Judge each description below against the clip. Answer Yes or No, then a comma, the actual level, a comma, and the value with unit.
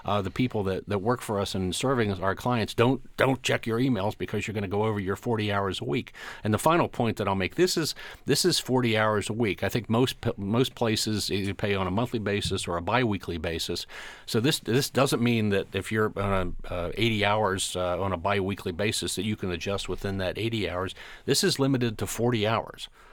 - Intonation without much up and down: No, average, 3.6 semitones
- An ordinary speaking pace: No, fast, 235 wpm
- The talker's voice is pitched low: Yes, low, 105 Hz